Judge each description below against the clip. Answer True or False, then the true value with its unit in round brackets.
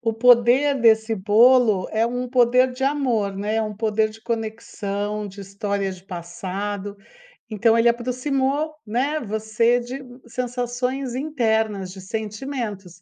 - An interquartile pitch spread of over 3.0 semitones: True (3.4 semitones)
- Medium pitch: False (225 Hz)